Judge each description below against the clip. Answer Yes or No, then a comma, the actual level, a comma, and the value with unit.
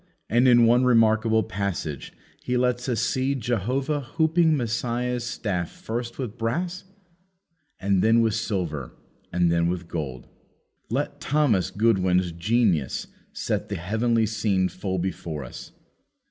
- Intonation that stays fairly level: No, average, 5.0 semitones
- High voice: No, low, 110 Hz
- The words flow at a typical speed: No, slow, 130 wpm